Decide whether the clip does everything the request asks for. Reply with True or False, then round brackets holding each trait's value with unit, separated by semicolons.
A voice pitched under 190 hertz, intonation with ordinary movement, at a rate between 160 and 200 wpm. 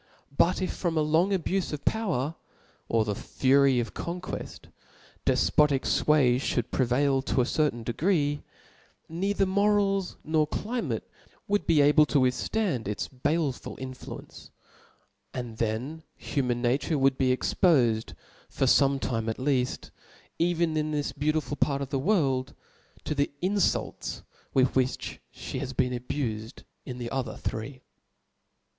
False (140 Hz; 4.4 semitones; 140 wpm)